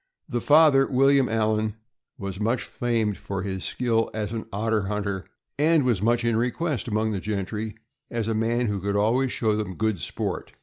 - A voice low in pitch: Yes, low, 110 Hz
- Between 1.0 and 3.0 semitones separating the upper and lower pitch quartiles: Yes, average, 2.7 semitones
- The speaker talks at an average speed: Yes, average, 180 wpm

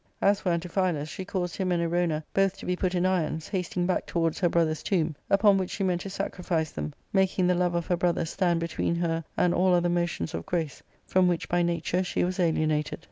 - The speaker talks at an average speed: No, fast, 225 wpm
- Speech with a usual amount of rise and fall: No, narrow, 1.9 semitones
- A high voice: No, medium, 175 Hz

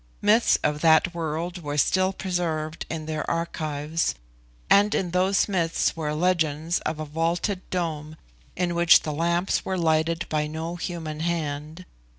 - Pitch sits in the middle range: Yes, medium, 165 Hz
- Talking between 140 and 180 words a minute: Yes, average, 150 wpm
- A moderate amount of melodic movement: No, narrow, 2.3 semitones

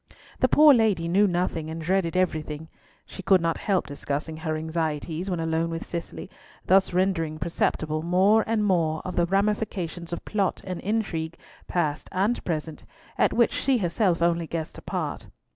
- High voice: No, medium, 170 Hz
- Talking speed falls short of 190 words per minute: Yes, average, 160 wpm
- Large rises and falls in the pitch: No, average, 3.3 semitones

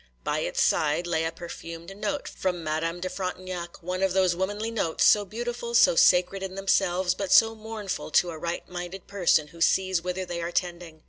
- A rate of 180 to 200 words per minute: Yes, average, 190 wpm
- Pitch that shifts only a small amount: Yes, narrow, 2.2 semitones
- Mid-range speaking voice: Yes, medium, 180 Hz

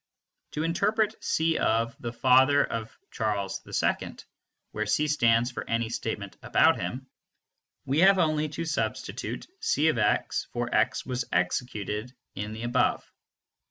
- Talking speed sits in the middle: No, slow, 130 wpm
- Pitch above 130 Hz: No, low, 125 Hz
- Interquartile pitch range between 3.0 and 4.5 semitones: No, wide, 5.6 semitones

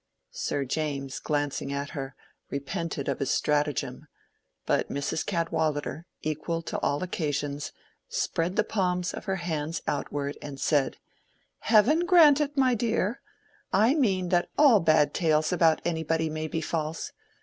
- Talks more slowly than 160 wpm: Yes, slow, 135 wpm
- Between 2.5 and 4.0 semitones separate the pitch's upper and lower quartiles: No, average, 4.4 semitones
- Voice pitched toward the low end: No, medium, 160 Hz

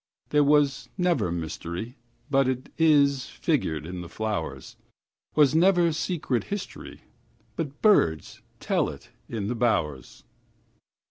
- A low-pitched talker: Yes, low, 130 Hz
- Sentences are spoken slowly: Yes, slow, 95 wpm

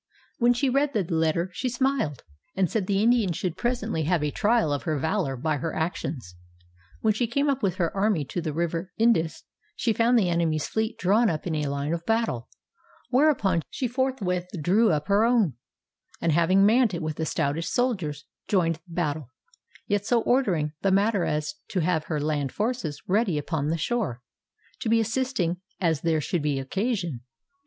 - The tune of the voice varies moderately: No, wide, 6.3 semitones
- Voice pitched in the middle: Yes, medium, 180 Hz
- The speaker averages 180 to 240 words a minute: Yes, average, 185 wpm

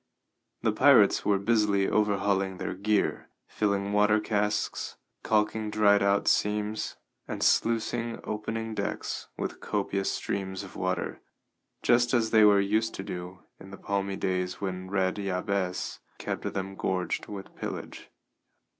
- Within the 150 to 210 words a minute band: No, slow, 135 wpm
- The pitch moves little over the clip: Yes, narrow, 1.8 semitones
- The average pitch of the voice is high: No, low, 100 Hz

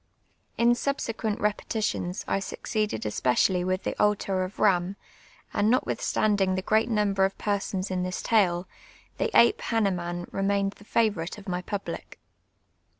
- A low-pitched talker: No, high, 195 Hz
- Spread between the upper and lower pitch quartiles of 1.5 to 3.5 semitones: Yes, narrow, 2.5 semitones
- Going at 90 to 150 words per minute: Yes, average, 140 wpm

